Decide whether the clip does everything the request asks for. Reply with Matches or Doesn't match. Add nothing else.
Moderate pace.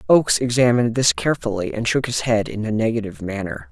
Matches